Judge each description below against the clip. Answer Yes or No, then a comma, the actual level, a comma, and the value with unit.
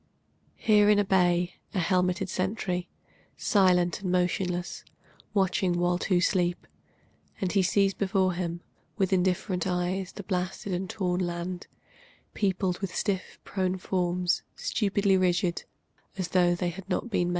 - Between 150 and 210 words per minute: No, average, 140 wpm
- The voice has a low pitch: No, medium, 185 Hz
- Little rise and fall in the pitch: Yes, narrow, 1.4 semitones